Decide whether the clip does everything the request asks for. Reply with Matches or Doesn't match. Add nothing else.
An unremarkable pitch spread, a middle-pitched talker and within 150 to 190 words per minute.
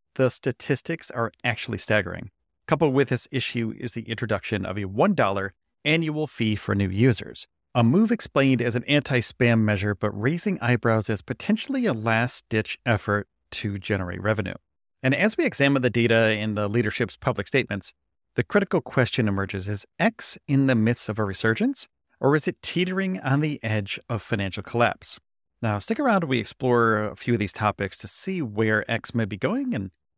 Doesn't match